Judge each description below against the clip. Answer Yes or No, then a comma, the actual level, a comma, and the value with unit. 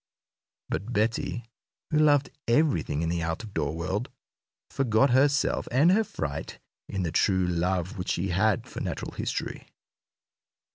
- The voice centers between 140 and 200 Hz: No, low, 100 Hz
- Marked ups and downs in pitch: Yes, wide, 7.4 semitones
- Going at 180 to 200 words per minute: No, average, 145 wpm